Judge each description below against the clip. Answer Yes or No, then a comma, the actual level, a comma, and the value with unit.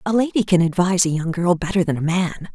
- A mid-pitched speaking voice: Yes, medium, 180 Hz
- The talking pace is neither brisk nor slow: No, fast, 260 wpm